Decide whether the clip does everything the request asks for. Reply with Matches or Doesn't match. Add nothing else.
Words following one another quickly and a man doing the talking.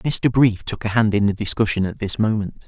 Matches